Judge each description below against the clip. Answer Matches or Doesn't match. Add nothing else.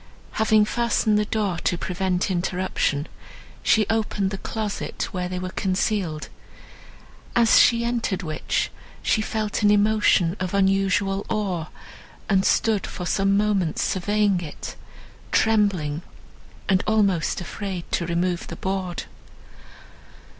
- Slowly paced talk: Matches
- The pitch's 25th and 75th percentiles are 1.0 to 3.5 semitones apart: Matches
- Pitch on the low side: Doesn't match